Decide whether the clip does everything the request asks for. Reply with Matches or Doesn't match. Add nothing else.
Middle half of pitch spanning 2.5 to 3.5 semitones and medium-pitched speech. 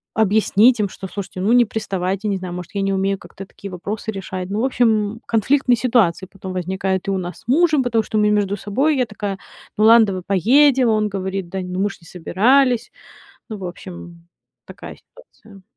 Doesn't match